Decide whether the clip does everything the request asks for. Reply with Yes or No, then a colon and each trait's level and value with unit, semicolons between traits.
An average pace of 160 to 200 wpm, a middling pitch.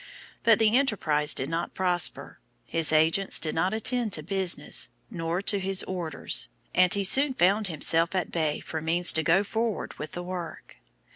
Yes: average, 170 wpm; medium, 180 Hz